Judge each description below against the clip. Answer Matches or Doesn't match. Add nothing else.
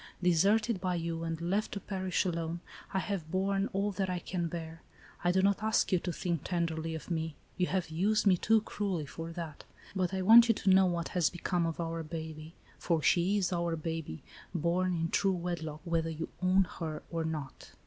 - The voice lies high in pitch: Doesn't match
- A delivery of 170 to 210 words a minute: Matches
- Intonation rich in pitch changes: Doesn't match